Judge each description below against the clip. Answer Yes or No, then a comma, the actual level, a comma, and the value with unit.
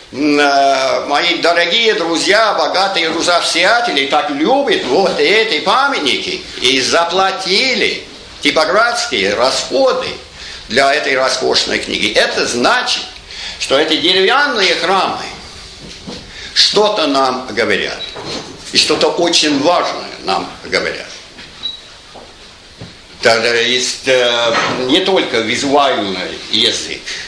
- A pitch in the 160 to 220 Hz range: Yes, high, 190 Hz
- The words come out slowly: Yes, slow, 85 wpm